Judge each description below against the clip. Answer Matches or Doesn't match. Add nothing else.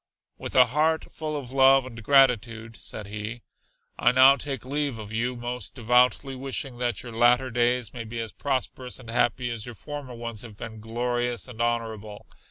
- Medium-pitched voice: Doesn't match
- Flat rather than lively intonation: Matches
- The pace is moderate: Matches